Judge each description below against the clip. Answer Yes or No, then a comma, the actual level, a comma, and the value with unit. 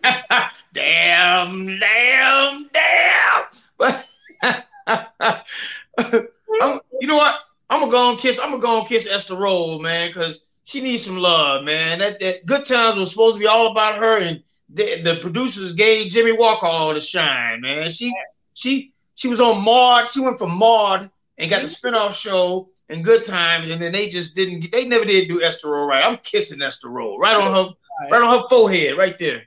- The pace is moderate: Yes, average, 185 wpm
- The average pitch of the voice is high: Yes, high, 220 Hz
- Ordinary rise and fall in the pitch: No, wide, 5.8 semitones